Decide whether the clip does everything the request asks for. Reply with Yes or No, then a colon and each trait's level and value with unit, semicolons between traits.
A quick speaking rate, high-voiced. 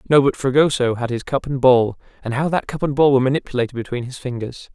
No: fast, 240 wpm; low, 130 Hz